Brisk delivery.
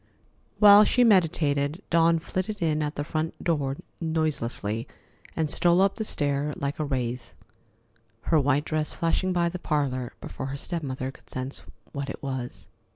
No: average, 160 wpm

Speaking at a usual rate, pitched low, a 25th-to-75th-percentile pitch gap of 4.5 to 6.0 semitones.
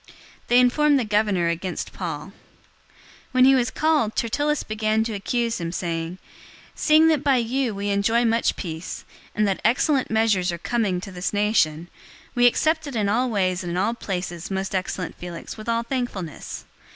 No: average, 180 wpm; high, 215 Hz; average, 4.9 semitones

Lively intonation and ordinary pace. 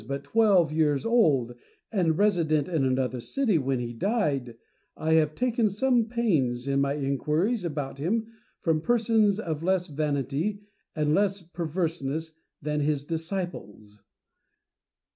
No: wide, 6.3 semitones; slow, 130 wpm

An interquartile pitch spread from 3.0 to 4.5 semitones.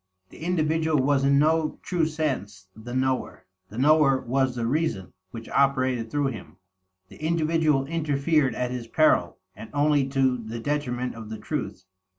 Yes: average, 4.0 semitones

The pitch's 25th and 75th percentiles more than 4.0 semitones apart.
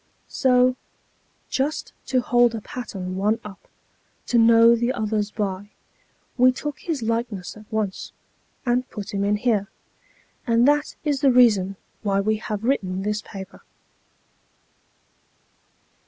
No: average, 3.5 semitones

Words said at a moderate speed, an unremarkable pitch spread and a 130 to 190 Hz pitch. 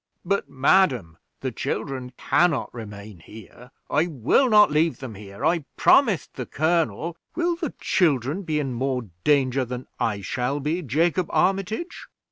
No: average, 155 wpm; wide, 5.9 semitones; medium, 140 Hz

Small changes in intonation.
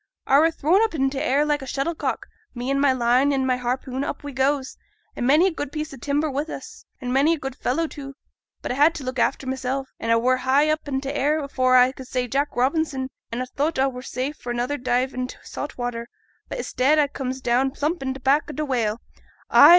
Yes: narrow, 2.3 semitones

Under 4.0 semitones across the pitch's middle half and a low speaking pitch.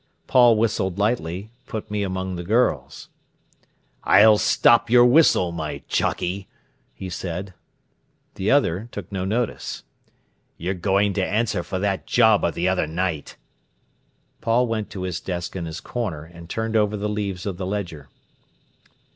Yes: average, 3.5 semitones; low, 100 Hz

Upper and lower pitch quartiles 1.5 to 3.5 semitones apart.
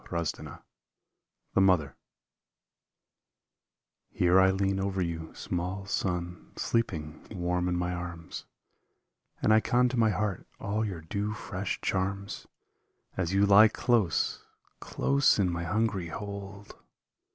Yes: average, 2.7 semitones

